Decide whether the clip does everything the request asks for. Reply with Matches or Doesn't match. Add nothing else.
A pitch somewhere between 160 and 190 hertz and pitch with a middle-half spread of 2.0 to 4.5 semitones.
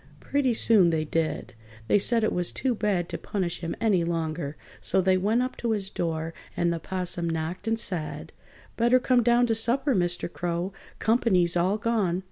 Doesn't match